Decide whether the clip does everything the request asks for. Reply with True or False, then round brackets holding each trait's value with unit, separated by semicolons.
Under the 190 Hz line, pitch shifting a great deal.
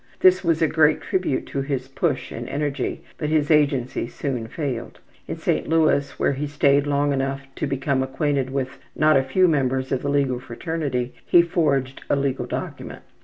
False (140 Hz; 2.4 semitones)